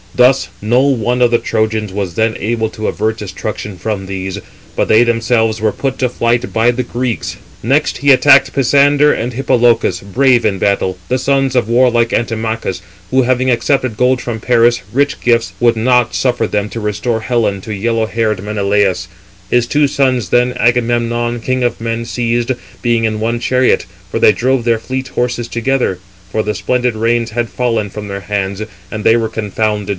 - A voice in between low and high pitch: No, low, 115 Hz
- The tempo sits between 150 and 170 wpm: No, average, 180 wpm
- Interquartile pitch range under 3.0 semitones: Yes, narrow, 2.4 semitones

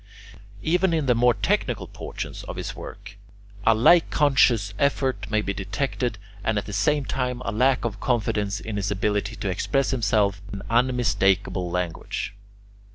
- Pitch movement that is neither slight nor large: Yes, average, 4.3 semitones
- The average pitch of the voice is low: Yes, low, 110 Hz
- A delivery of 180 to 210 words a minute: No, average, 160 wpm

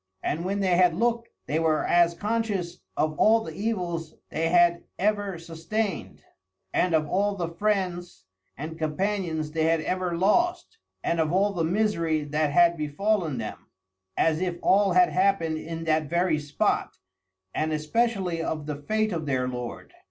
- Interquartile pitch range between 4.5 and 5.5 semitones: No, average, 4.0 semitones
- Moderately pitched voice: Yes, medium, 170 Hz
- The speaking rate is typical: Yes, average, 160 wpm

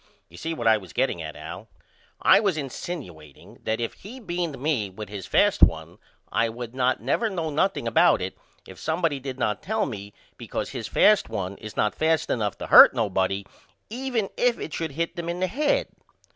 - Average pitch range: No, wide, 8.7 semitones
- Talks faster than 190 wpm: Yes, average, 200 wpm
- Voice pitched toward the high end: No, low, 135 Hz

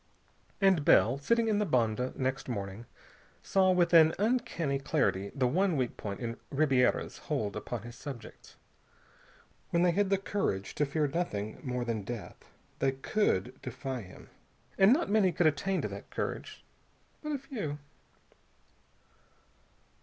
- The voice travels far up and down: Yes, wide, 7.8 semitones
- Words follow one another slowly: No, average, 145 wpm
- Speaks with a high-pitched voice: No, medium, 140 Hz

